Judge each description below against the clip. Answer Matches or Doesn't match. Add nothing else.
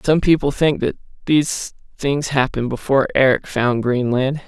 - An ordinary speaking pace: Matches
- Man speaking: Matches